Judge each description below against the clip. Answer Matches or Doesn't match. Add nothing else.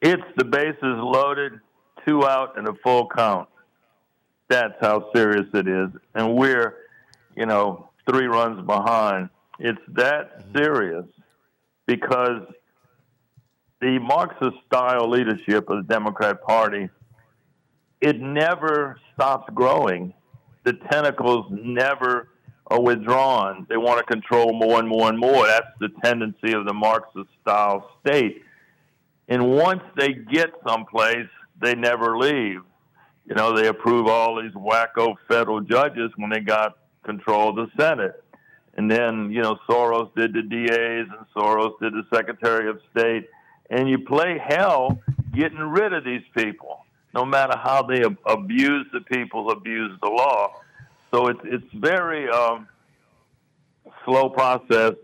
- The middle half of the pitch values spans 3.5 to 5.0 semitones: Doesn't match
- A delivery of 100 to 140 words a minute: Matches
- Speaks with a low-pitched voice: Matches